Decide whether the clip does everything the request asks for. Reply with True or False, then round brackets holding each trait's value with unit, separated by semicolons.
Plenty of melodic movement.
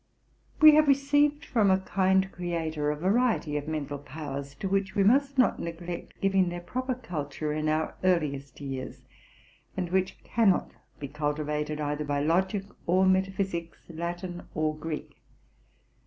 False (4.3 semitones)